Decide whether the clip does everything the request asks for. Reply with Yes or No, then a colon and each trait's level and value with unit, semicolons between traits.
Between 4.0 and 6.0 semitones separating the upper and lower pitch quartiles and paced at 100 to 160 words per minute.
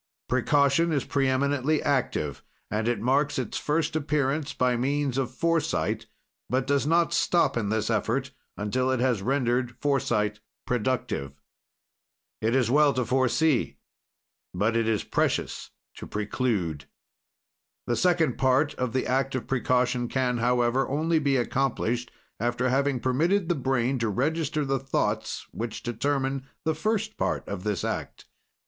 No: average, 3.0 semitones; average, 140 wpm